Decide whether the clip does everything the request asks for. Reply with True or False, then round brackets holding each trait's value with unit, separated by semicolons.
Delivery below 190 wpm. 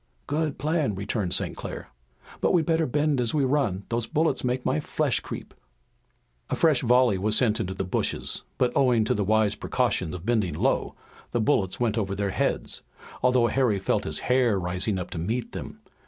False (195 wpm)